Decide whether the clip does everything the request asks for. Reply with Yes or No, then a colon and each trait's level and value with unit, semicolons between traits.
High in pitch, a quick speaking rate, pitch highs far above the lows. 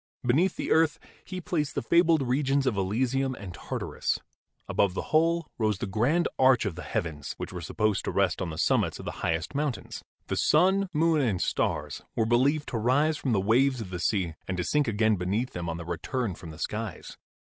No: low, 120 Hz; fast, 210 wpm; wide, 7.7 semitones